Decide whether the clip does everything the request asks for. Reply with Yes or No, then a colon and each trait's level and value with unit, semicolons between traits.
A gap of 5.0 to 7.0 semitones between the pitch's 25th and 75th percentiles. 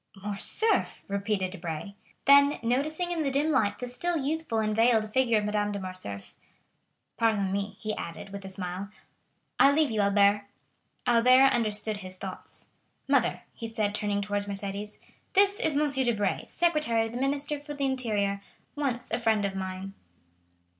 Yes: wide, 5.4 semitones